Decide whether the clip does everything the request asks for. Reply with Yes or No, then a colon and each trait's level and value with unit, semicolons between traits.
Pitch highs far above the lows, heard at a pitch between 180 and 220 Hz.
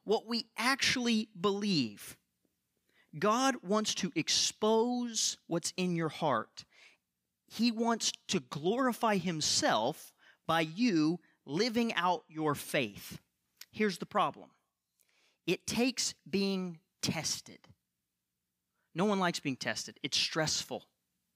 Yes: wide, 5.9 semitones; high, 190 Hz